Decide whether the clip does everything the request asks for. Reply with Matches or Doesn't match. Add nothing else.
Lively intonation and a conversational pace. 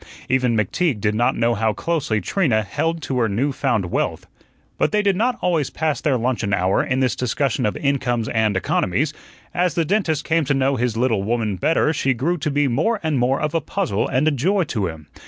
Doesn't match